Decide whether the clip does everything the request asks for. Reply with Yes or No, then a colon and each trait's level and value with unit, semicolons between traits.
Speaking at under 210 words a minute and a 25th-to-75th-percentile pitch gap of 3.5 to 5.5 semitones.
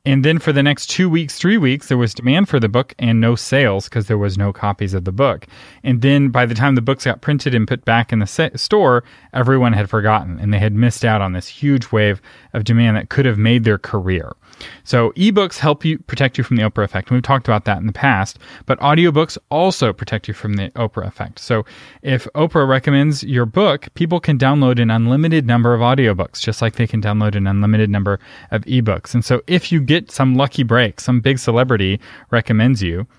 No: fast, 225 wpm; average, 4.1 semitones